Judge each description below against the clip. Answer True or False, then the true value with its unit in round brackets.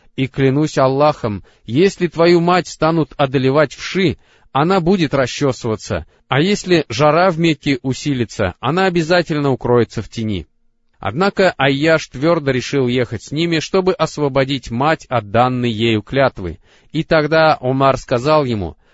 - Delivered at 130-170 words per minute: True (135 wpm)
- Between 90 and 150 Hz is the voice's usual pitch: True (140 Hz)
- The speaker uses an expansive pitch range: False (5.0 semitones)